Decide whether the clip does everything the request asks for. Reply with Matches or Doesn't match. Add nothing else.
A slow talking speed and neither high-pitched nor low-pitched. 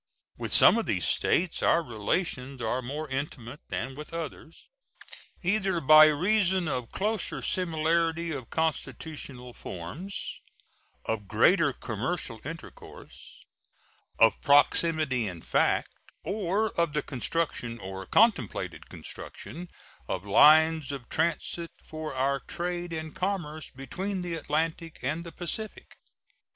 Matches